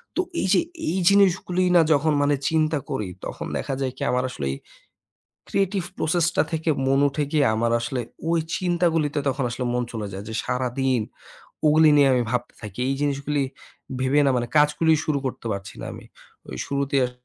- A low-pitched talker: No, medium, 145 Hz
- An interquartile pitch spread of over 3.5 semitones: Yes, average, 4.2 semitones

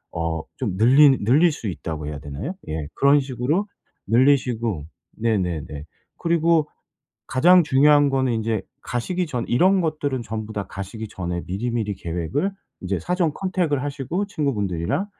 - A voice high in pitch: No, low, 125 Hz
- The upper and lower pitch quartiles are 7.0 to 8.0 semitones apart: Yes, wide, 7.7 semitones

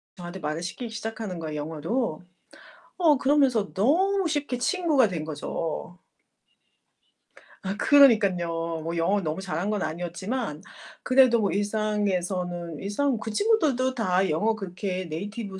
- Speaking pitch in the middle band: No, high, 200 Hz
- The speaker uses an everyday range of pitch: No, wide, 6.3 semitones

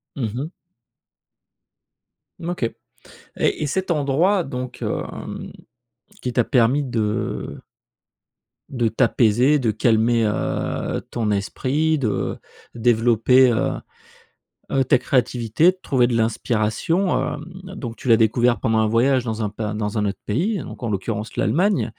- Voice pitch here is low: Yes, low, 120 Hz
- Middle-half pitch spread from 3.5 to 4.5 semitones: Yes, average, 3.8 semitones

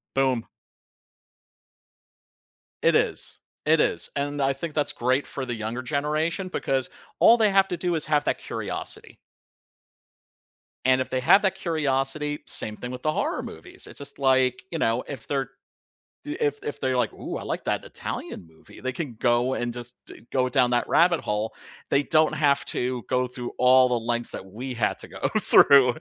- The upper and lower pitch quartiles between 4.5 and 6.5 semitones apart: No, average, 3.2 semitones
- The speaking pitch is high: No, low, 130 Hz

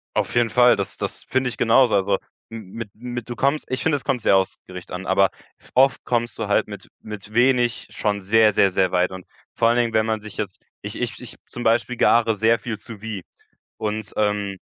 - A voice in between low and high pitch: No, low, 110 Hz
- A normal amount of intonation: Yes, average, 3.1 semitones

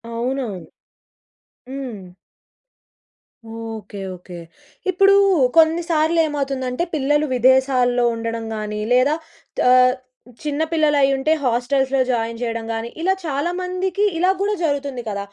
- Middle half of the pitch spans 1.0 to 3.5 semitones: No, average, 4.9 semitones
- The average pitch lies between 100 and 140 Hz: No, very high, 265 Hz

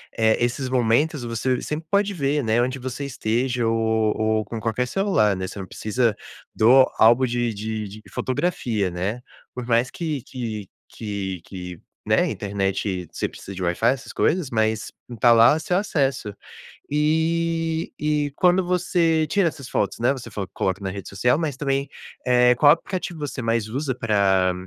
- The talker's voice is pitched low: Yes, low, 120 Hz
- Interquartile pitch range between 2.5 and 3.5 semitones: No, average, 5.3 semitones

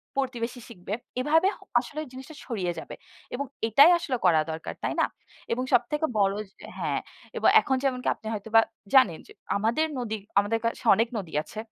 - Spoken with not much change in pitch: No, average, 4.6 semitones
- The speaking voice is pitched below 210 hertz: No, high, 235 Hz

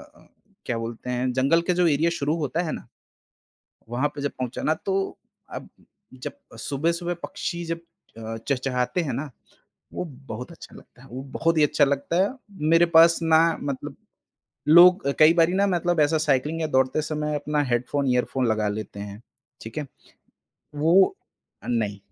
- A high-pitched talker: No, medium, 145 Hz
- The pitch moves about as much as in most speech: Yes, average, 4.8 semitones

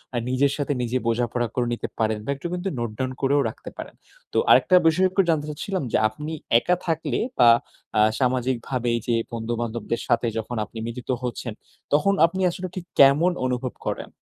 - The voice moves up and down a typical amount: Yes, average, 4.9 semitones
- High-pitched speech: No, low, 130 Hz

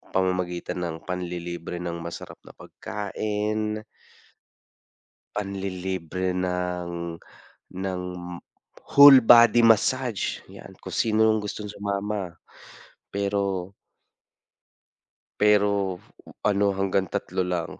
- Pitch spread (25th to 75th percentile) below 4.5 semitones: Yes, average, 2.7 semitones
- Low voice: Yes, very low, 95 Hz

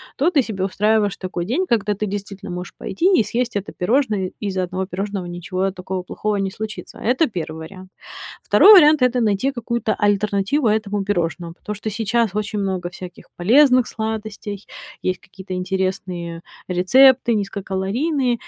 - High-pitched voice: Yes, high, 205 Hz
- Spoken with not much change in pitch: No, average, 3.7 semitones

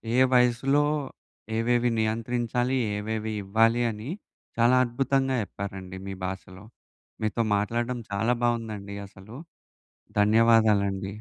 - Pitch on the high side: No, low, 115 Hz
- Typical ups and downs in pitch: Yes, average, 3.2 semitones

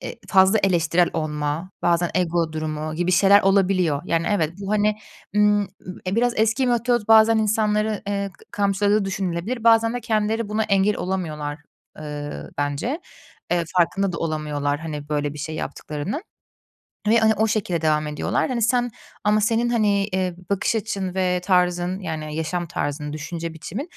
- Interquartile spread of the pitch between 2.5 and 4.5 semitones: No, average, 4.9 semitones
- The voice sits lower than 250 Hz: Yes, high, 190 Hz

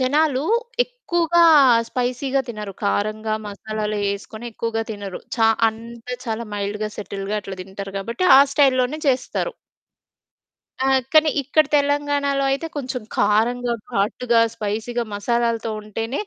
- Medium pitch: No, high, 235 Hz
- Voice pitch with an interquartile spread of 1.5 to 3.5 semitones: No, average, 4.3 semitones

